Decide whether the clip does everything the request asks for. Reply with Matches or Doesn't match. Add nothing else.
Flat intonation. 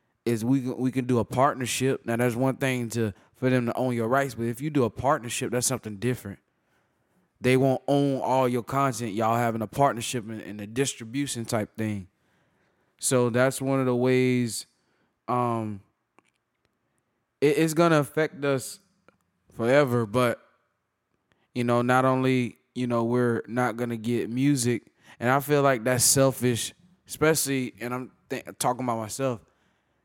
Matches